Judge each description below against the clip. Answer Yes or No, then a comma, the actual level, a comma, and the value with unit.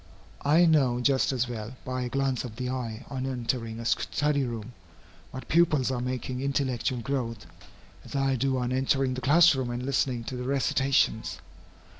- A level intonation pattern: Yes, narrow, 1.9 semitones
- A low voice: Yes, low, 130 Hz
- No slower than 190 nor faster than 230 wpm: No, average, 175 wpm